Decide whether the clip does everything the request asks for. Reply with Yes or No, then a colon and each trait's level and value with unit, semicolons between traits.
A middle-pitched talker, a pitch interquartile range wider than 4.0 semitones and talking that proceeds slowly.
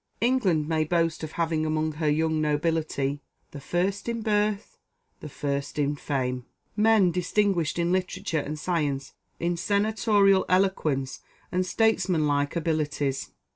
Yes: medium, 165 Hz; average, 4.4 semitones; slow, 130 wpm